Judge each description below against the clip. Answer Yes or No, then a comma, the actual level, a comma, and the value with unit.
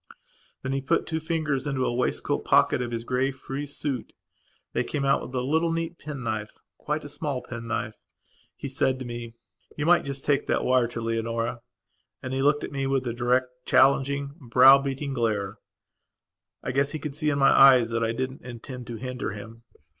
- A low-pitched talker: Yes, low, 130 Hz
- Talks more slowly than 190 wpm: No, average, 200 wpm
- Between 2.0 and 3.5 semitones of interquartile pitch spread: Yes, average, 2.9 semitones